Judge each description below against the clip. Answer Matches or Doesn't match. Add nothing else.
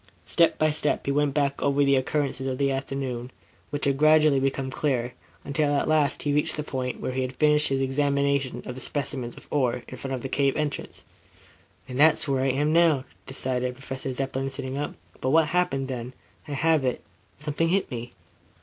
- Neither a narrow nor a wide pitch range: Doesn't match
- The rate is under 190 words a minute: Doesn't match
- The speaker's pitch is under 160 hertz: Matches